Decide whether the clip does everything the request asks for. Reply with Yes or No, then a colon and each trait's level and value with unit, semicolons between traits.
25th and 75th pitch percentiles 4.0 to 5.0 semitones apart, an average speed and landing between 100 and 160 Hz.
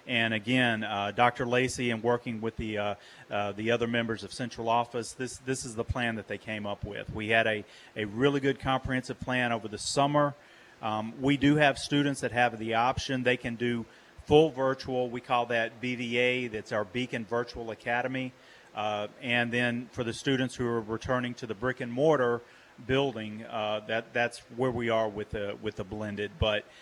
No: narrow, 2.5 semitones; average, 195 wpm; low, 120 Hz